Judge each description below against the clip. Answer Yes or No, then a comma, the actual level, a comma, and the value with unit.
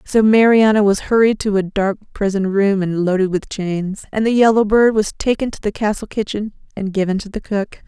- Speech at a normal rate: No, fast, 215 wpm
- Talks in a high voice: Yes, high, 205 Hz